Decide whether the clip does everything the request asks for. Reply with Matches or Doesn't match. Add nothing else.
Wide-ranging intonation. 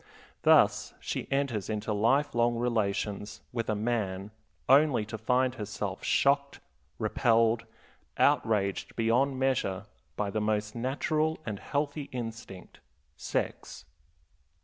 Doesn't match